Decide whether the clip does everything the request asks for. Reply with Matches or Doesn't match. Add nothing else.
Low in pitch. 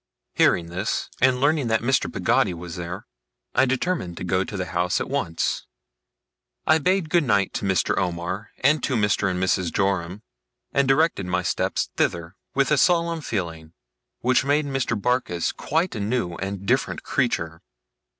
Matches